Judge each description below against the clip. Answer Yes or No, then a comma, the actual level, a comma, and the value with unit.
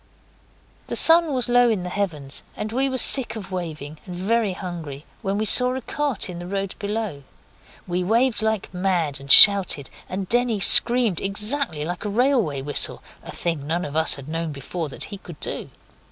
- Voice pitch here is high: Yes, high, 195 Hz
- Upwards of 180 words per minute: Yes, average, 190 wpm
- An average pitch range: No, wide, 5.8 semitones